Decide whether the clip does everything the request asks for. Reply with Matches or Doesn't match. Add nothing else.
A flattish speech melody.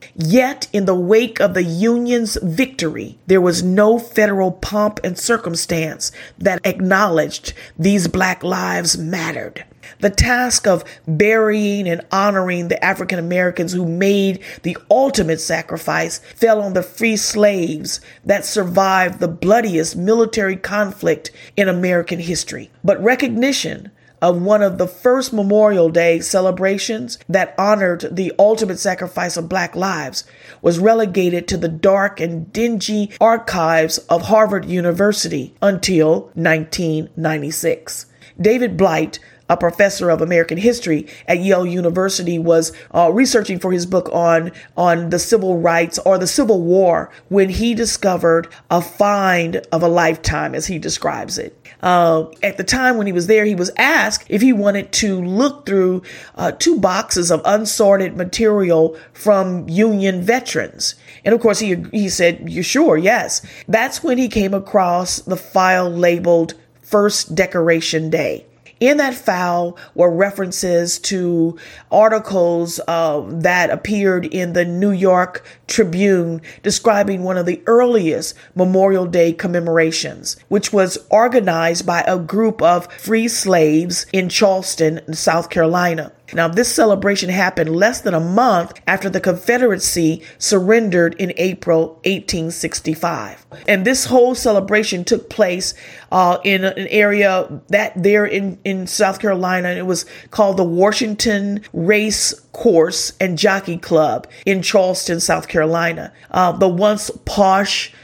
Doesn't match